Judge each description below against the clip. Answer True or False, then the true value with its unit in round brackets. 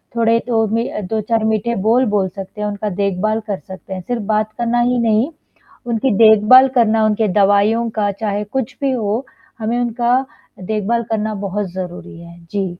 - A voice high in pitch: True (215 Hz)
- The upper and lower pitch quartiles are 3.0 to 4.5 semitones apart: False (2.4 semitones)